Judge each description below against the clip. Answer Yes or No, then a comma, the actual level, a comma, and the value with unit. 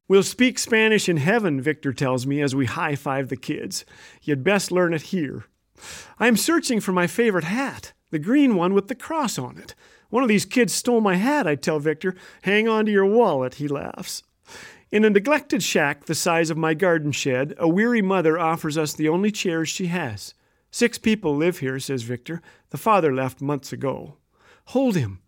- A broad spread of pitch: Yes, wide, 7.1 semitones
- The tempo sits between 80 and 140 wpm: No, average, 200 wpm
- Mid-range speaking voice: Yes, medium, 175 Hz